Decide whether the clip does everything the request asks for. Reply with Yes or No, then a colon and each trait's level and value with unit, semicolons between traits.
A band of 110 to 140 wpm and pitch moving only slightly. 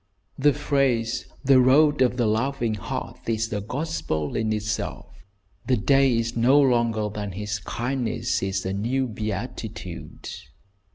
No: slow, 135 wpm; average, 3.9 semitones